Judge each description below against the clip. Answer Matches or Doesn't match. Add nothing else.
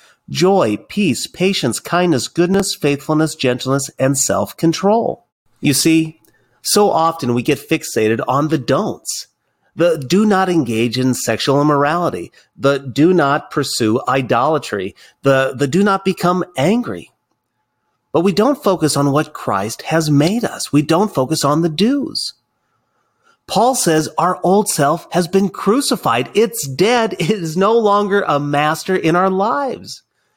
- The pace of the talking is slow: Doesn't match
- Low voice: Doesn't match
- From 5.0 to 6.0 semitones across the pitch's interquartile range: Matches